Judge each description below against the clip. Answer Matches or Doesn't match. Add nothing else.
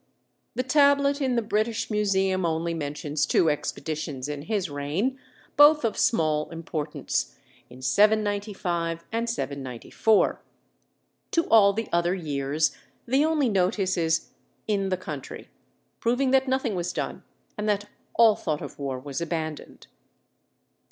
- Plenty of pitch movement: Matches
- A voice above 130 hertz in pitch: Matches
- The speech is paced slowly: Matches